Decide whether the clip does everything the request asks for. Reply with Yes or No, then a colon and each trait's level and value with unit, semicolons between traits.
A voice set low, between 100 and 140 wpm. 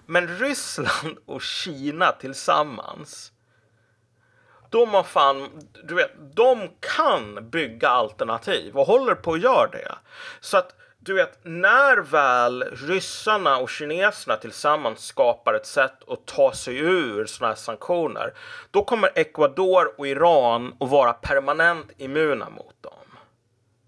No: medium, 180 Hz; slow, 125 wpm